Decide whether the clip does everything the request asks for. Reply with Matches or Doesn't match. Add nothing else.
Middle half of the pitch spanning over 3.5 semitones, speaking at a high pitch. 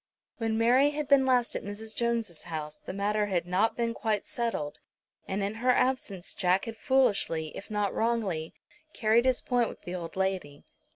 Matches